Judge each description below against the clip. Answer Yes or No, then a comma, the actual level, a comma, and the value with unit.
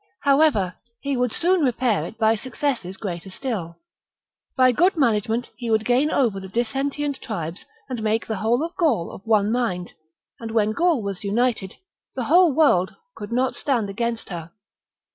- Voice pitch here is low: No, high, 230 Hz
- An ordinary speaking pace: Yes, average, 165 wpm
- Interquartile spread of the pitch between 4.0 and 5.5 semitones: Yes, average, 4.7 semitones